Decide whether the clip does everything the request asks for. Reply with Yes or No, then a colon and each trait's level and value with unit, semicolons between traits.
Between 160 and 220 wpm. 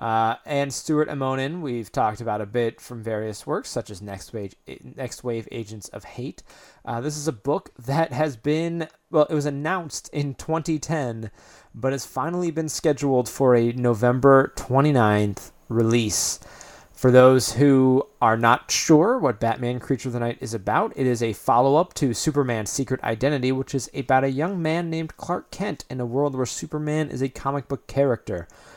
Yes: average, 180 wpm